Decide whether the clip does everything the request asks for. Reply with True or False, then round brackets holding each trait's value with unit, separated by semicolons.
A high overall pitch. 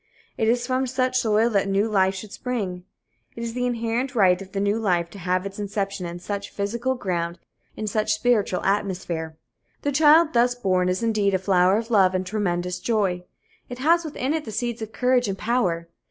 True (210 Hz)